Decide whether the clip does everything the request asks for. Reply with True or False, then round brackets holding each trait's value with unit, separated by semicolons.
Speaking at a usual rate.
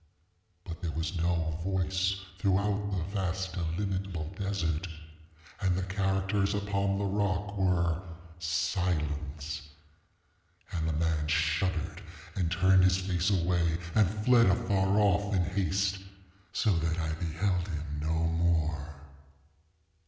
False (120 wpm)